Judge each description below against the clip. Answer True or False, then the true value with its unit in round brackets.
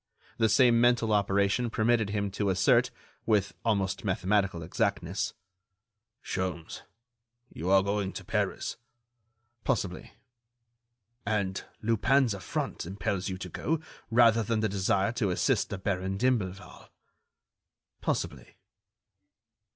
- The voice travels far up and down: False (3.1 semitones)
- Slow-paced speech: True (110 wpm)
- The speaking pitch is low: True (100 Hz)